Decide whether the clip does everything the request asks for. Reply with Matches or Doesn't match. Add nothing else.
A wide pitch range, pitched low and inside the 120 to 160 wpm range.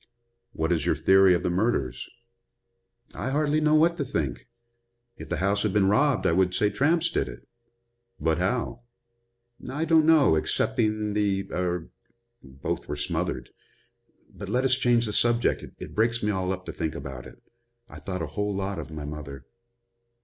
Doesn't match